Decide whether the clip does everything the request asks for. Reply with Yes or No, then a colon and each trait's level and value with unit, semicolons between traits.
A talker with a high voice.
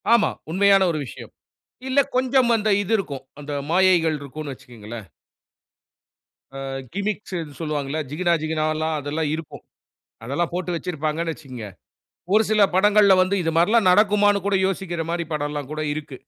No: medium, 165 Hz